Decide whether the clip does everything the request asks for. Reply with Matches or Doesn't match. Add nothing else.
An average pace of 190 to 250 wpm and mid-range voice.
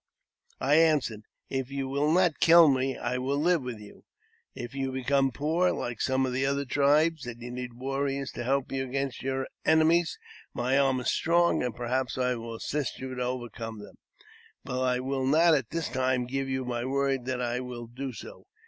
Doesn't match